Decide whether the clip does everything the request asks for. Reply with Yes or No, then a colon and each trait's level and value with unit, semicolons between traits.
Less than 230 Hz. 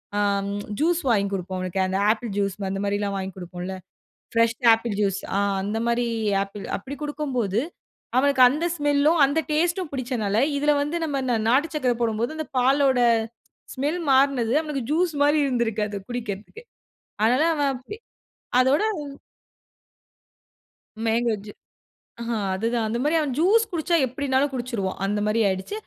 No: high, 245 Hz